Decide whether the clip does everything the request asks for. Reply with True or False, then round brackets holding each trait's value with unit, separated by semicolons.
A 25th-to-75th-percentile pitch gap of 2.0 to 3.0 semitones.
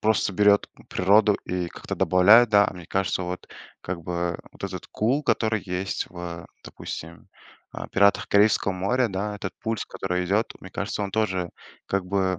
True (2.4 semitones)